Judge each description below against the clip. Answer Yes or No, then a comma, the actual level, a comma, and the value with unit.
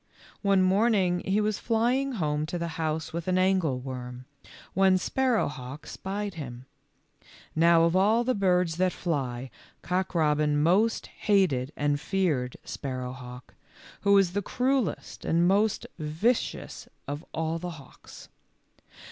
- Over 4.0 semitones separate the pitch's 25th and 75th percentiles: Yes, average, 5.1 semitones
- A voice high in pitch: No, medium, 170 Hz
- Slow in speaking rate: Yes, slow, 130 wpm